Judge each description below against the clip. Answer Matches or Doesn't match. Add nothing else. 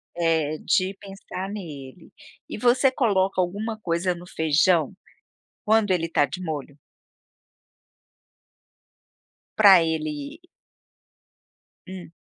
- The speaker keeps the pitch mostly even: Doesn't match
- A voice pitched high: Doesn't match